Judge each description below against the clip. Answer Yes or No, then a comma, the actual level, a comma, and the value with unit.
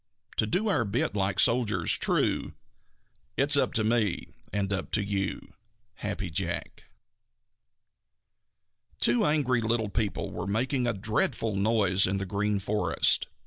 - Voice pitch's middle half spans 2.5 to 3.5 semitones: Yes, average, 3.1 semitones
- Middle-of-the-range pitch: No, low, 105 Hz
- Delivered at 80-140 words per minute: Yes, slow, 135 wpm